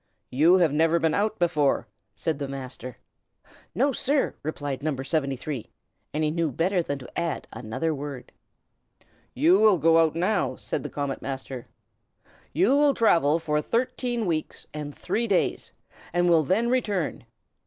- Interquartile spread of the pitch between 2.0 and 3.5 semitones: No, average, 4.8 semitones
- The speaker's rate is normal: Yes, average, 155 wpm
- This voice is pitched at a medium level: Yes, medium, 160 Hz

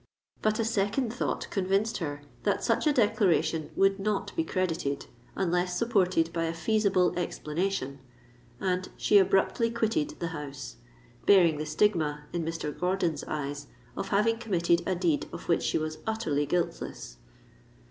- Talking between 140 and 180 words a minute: Yes, average, 145 wpm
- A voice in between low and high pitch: Yes, medium, 180 Hz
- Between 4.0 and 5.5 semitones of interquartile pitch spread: Yes, average, 4.6 semitones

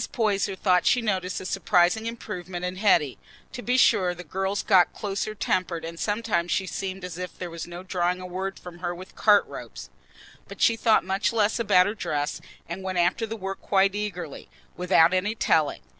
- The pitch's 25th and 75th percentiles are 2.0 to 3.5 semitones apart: Yes, average, 2.7 semitones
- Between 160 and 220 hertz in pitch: Yes, medium, 185 Hz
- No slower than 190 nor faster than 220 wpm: Yes, average, 195 wpm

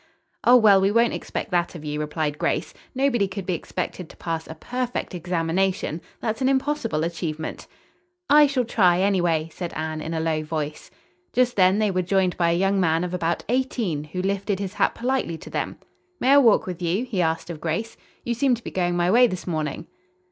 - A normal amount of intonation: No, wide, 5.7 semitones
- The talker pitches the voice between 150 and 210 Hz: Yes, medium, 185 Hz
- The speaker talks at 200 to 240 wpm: Yes, fast, 205 wpm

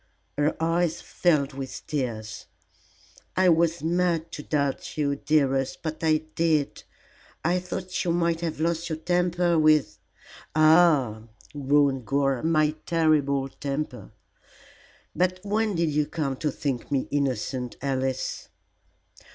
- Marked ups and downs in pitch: No, average, 3.5 semitones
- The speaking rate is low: Yes, slow, 125 wpm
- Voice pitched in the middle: Yes, medium, 155 Hz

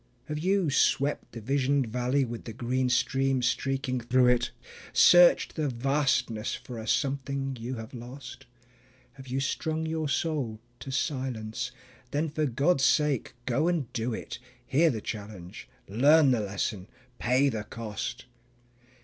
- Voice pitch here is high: No, low, 130 Hz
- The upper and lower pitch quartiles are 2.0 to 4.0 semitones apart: Yes, average, 3.1 semitones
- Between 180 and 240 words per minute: No, average, 145 wpm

